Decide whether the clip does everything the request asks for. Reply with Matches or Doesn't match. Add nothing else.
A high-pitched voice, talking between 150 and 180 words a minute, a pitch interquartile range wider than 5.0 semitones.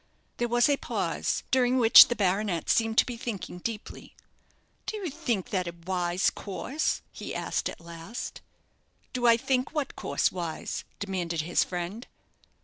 Matches